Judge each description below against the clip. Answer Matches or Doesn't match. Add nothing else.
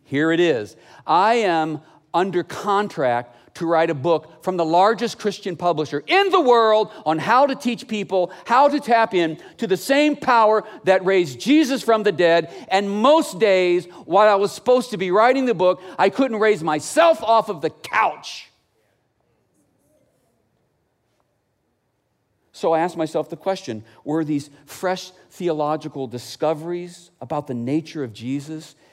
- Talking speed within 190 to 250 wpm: Doesn't match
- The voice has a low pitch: Doesn't match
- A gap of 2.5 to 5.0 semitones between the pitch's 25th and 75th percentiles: Doesn't match